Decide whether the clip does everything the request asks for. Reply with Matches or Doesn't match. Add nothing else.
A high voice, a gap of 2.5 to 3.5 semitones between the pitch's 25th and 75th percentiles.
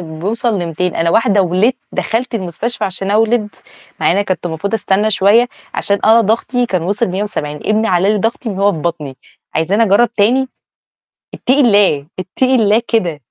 Doesn't match